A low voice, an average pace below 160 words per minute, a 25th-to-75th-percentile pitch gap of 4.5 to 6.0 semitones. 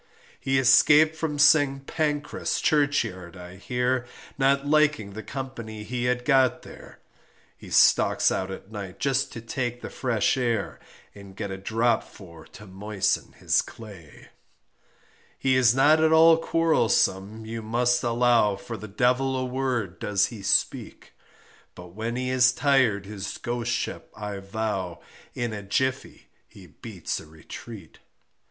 Yes: low, 120 Hz; average, 145 wpm; average, 4.8 semitones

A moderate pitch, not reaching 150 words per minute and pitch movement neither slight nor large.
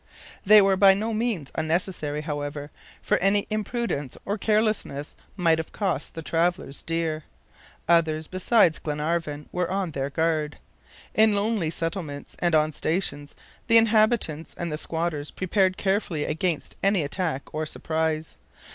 Yes: medium, 165 Hz; average, 140 wpm; average, 4.4 semitones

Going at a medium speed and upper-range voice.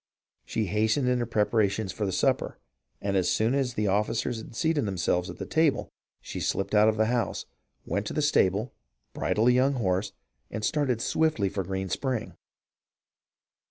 No: average, 165 wpm; low, 110 Hz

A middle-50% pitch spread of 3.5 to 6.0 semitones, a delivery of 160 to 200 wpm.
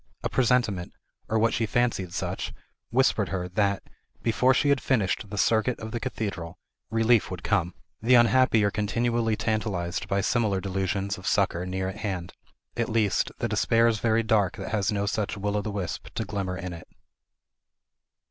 No: average, 3.1 semitones; average, 175 wpm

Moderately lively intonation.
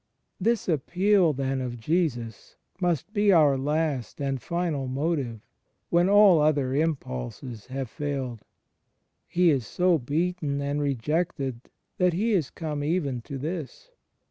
Yes: average, 4.7 semitones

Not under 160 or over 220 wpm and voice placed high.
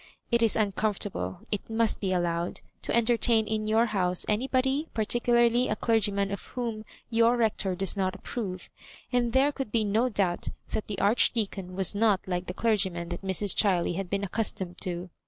Yes: average, 175 wpm; high, 210 Hz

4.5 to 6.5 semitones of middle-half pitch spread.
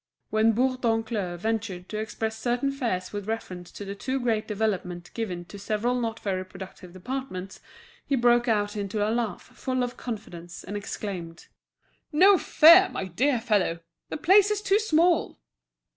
Yes: average, 4.8 semitones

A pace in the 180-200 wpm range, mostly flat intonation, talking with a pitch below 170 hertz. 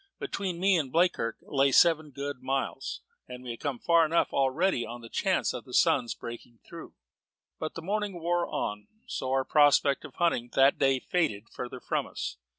No: average, 190 wpm; average, 5.1 semitones; medium, 140 Hz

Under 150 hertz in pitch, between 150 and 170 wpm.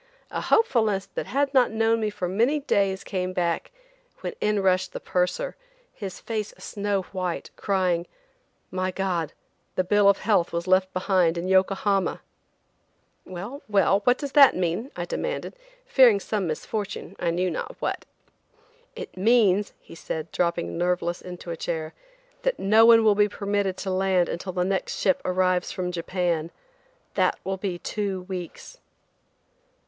No: high, 190 Hz; average, 155 wpm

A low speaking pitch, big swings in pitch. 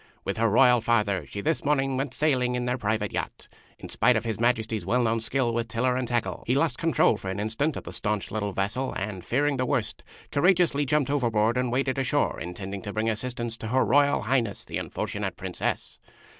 No: low, 120 Hz; average, 3.7 semitones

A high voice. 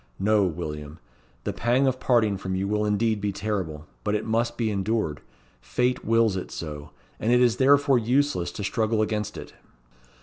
No: low, 110 Hz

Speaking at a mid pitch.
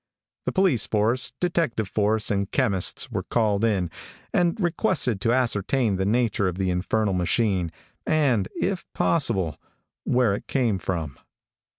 No: low, 110 Hz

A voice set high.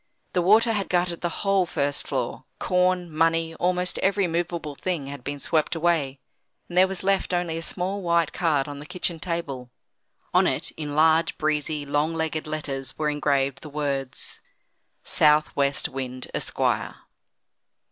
No: medium, 160 Hz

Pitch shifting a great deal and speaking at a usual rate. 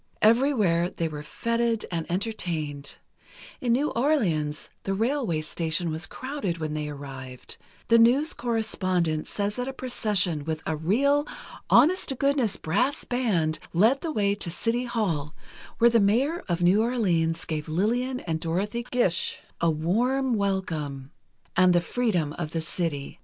Yes: wide, 7.0 semitones; average, 150 wpm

